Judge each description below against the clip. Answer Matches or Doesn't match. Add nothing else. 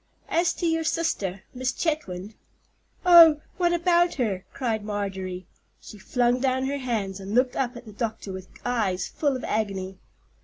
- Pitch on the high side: Matches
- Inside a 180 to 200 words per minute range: Doesn't match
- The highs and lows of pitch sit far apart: Matches